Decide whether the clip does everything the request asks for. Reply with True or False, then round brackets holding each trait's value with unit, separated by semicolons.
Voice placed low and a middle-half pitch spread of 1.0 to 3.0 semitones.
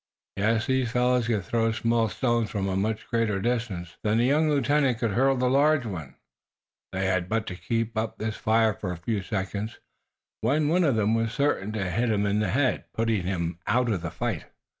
False (110 Hz; 3.7 semitones)